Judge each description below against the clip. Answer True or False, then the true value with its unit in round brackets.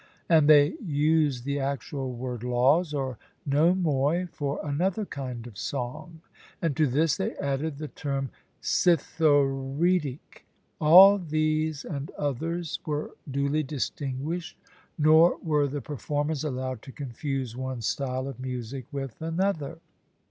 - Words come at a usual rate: False (125 wpm)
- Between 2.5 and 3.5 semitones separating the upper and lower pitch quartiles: True (3.0 semitones)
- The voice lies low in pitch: False (145 Hz)